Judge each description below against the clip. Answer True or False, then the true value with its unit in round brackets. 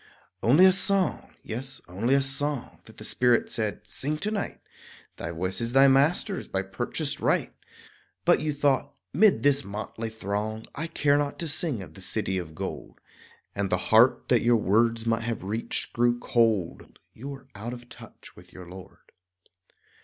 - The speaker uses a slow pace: False (175 wpm)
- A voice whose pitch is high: False (120 Hz)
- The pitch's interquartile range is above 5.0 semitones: True (5.5 semitones)